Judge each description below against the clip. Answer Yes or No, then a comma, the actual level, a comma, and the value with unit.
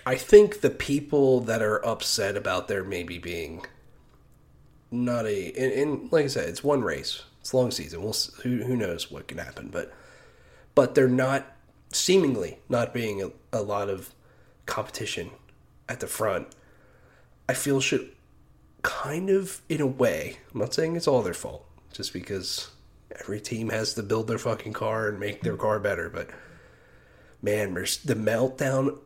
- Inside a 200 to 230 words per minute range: No, average, 165 wpm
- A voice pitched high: No, low, 125 Hz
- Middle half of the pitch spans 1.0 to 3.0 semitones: No, average, 4.3 semitones